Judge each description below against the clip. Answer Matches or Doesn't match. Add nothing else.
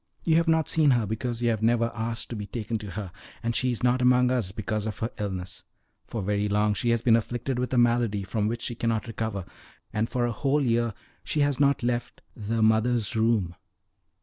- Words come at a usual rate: Doesn't match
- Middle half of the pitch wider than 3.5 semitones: Doesn't match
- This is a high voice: Doesn't match